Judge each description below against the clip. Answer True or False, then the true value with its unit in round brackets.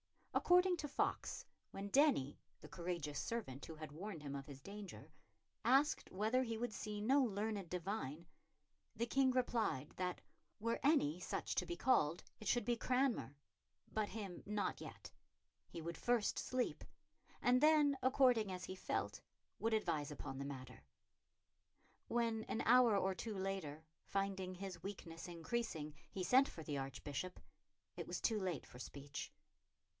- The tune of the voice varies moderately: False (6.6 semitones)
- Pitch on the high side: True (200 Hz)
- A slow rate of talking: False (155 wpm)